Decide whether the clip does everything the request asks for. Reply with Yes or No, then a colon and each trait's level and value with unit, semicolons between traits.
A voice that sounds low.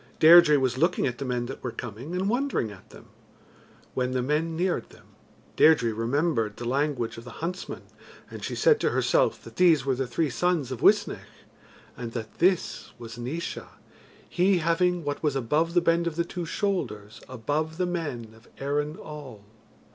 No: medium, 145 Hz